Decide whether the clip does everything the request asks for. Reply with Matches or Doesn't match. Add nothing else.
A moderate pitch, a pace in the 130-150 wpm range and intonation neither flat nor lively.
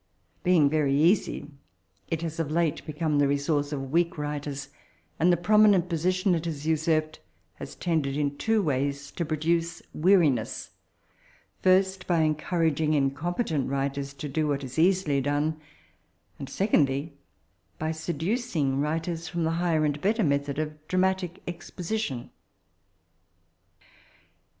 Matches